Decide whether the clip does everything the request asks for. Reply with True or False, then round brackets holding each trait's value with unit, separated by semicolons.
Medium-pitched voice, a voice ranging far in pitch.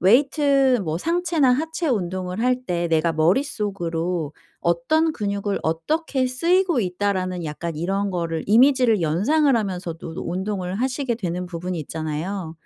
False (195 Hz; 7.2 semitones)